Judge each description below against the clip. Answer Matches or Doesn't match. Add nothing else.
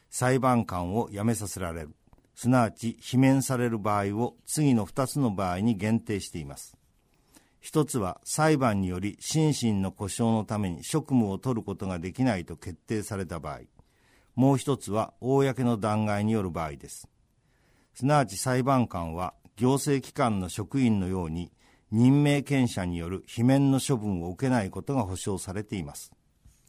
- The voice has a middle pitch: Doesn't match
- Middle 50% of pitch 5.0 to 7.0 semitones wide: Matches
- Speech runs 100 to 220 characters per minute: Doesn't match